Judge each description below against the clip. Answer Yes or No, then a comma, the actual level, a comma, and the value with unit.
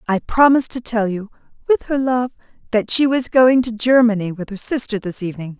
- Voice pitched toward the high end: Yes, high, 235 Hz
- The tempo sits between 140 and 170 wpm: No, fast, 205 wpm